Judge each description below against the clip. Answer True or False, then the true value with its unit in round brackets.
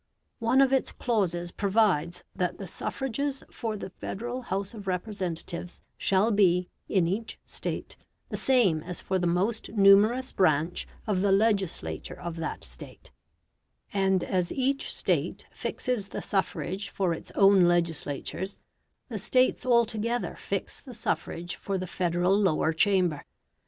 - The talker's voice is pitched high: True (195 Hz)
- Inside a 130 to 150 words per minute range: True (140 wpm)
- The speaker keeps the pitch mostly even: False (4.3 semitones)